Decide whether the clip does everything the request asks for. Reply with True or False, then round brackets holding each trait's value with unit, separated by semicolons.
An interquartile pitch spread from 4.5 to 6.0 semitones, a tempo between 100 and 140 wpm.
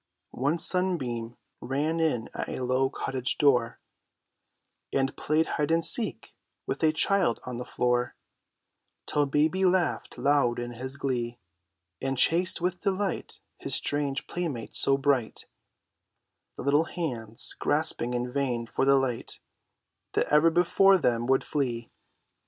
True (4.8 semitones; 135 wpm)